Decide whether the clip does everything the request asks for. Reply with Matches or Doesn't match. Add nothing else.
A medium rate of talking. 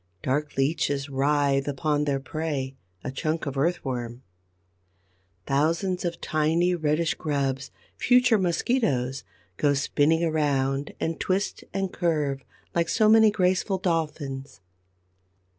Doesn't match